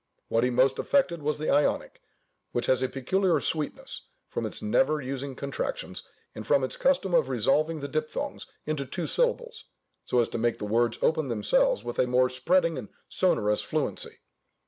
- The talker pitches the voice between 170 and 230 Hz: No, medium, 140 Hz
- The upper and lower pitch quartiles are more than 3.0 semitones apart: Yes, average, 4.7 semitones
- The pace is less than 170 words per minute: No, average, 175 wpm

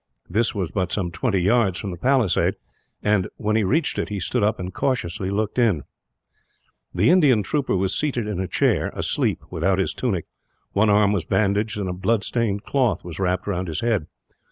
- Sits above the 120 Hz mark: No, low, 100 Hz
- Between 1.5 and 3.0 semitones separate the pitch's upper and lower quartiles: No, average, 3.7 semitones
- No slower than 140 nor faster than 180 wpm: No, average, 195 wpm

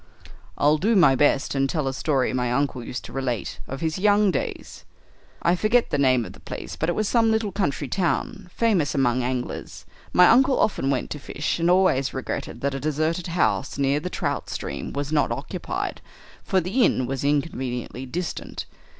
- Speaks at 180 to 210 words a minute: Yes, average, 190 wpm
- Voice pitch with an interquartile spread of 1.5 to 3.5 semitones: No, average, 5.2 semitones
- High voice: No, medium, 145 Hz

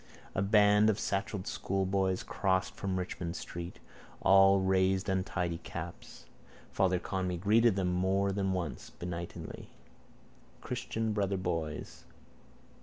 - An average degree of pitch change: No, narrow, 1.6 semitones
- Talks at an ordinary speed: No, slow, 110 wpm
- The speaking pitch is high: No, very low, 95 Hz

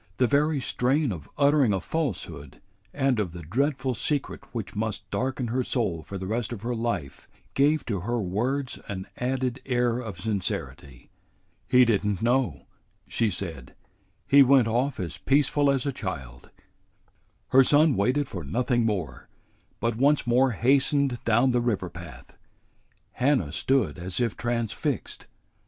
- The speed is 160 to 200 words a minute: No, average, 150 wpm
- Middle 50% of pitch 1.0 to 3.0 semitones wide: No, wide, 5.4 semitones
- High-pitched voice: No, low, 120 Hz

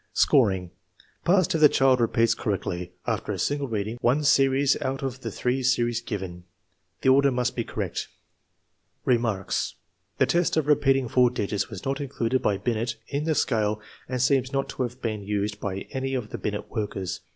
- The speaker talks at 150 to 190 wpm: Yes, average, 180 wpm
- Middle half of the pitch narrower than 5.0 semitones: Yes, average, 4.2 semitones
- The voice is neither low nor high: No, low, 125 Hz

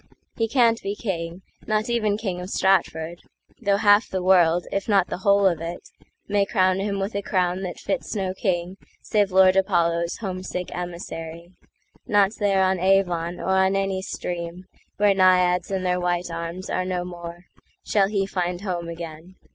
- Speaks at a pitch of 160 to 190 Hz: Yes, medium, 185 Hz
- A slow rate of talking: No, average, 155 wpm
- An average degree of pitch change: No, narrow, 2.0 semitones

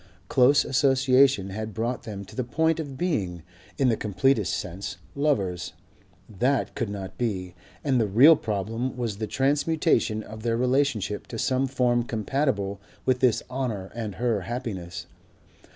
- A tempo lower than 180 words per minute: Yes, average, 150 wpm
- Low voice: Yes, low, 120 Hz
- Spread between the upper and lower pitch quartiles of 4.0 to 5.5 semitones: Yes, average, 4.6 semitones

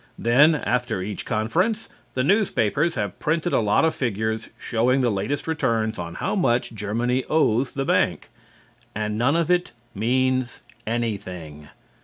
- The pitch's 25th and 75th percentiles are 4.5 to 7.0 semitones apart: Yes, average, 5.1 semitones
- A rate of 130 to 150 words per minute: Yes, average, 145 wpm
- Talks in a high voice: No, low, 120 Hz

